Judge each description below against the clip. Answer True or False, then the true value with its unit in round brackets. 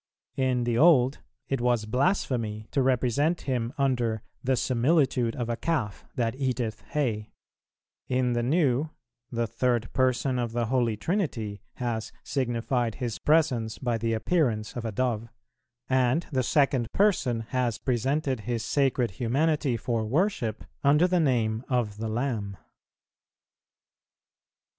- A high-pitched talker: False (125 Hz)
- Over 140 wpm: False (135 wpm)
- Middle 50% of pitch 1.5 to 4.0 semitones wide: True (3.0 semitones)